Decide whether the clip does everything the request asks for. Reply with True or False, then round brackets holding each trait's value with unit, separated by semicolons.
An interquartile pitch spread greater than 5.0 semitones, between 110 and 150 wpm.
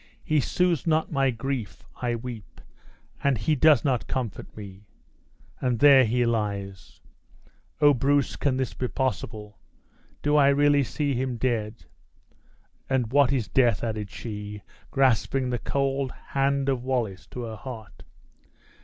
False (3.8 semitones; 140 wpm)